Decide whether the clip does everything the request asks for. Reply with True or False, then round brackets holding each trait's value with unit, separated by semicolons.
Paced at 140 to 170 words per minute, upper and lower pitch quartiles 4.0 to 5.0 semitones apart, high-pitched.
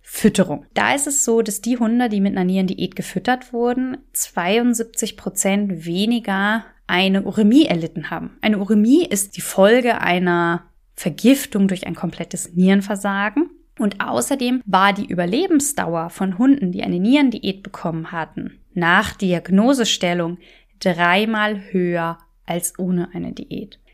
False (130 wpm; 4.6 semitones; 200 Hz)